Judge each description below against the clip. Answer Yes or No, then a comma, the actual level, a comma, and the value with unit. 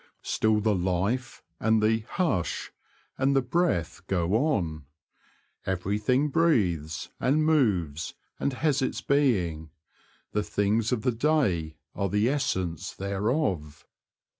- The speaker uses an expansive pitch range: Yes, wide, 7.0 semitones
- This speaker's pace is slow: Yes, slow, 115 wpm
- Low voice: Yes, low, 105 Hz